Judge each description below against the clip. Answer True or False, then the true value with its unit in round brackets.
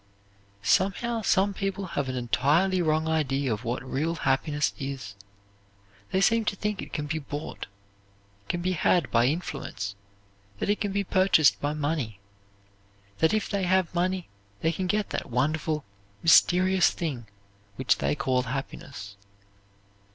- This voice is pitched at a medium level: True (160 Hz)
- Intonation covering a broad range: True (5.7 semitones)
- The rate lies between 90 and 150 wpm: True (145 wpm)